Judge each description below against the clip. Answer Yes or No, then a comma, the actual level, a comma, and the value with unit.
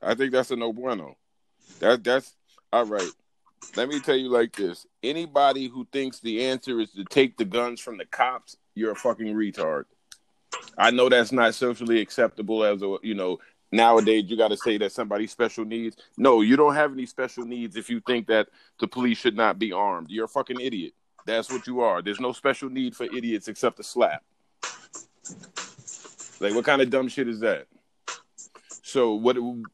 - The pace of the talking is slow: No, average, 195 wpm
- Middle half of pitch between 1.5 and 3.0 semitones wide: Yes, narrow, 2.5 semitones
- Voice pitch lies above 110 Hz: Yes, low, 120 Hz